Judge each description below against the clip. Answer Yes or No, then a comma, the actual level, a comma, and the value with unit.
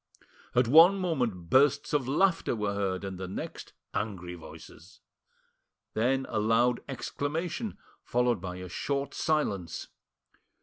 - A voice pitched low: Yes, low, 120 Hz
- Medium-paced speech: No, slow, 125 wpm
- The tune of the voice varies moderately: No, wide, 6.9 semitones